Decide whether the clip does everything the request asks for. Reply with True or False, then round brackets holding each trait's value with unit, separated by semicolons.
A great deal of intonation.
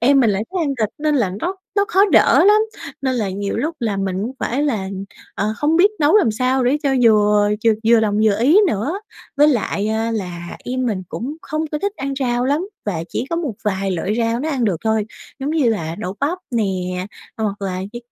True (6.0 semitones)